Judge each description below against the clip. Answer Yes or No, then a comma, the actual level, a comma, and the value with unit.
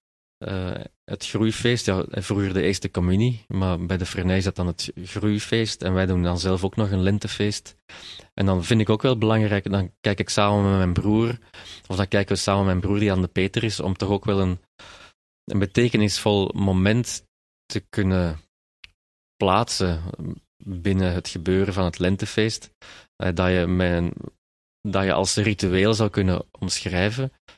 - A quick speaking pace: No, average, 175 wpm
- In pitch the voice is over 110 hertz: No, very low, 95 Hz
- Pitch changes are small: Yes, narrow, 2.3 semitones